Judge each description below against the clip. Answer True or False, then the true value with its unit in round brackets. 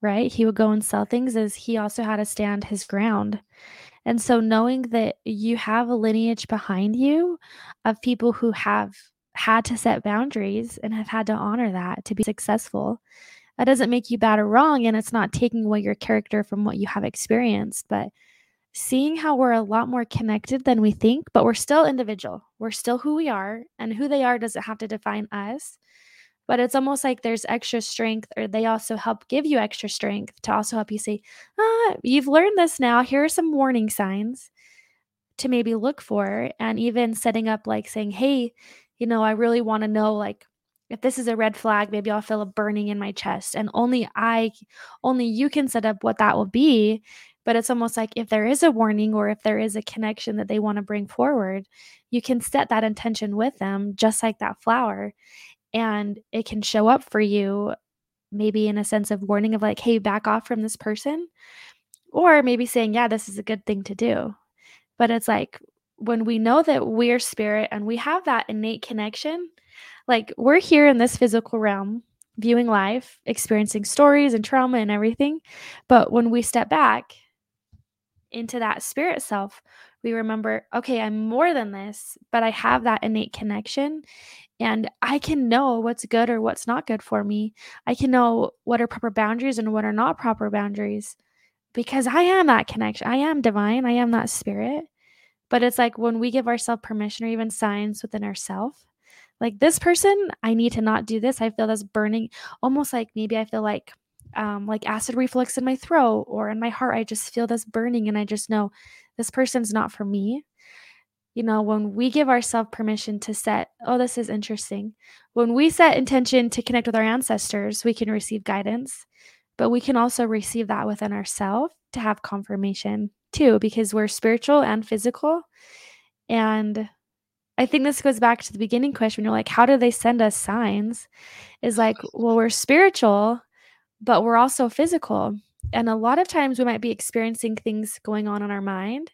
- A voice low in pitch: False (230 Hz)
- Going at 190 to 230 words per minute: True (200 wpm)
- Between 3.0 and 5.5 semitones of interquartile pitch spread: False (2.5 semitones)